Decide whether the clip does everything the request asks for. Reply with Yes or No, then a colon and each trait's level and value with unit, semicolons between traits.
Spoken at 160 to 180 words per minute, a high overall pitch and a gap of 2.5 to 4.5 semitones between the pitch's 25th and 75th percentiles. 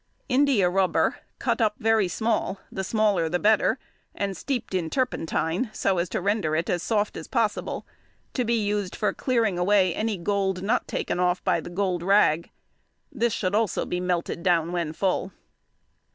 Yes: average, 165 wpm; high, 195 Hz; average, 3.4 semitones